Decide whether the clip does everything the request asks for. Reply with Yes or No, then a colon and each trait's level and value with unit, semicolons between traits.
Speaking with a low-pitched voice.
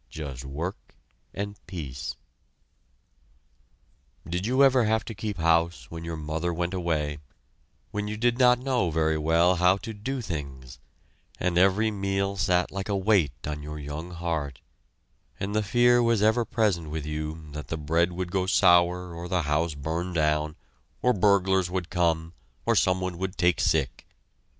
Yes: very low, 90 Hz